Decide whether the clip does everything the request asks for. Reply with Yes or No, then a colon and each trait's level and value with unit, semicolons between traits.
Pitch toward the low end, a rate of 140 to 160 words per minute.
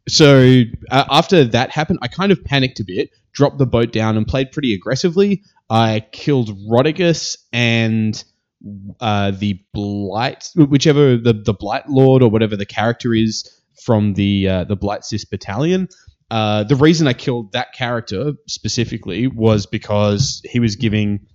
Yes: low, 115 Hz; average, 155 wpm